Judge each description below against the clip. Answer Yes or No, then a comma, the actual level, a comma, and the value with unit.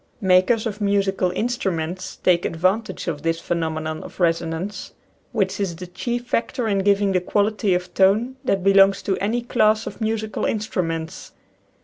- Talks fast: No, average, 150 wpm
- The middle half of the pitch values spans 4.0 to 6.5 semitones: No, average, 3.4 semitones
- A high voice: Yes, high, 195 Hz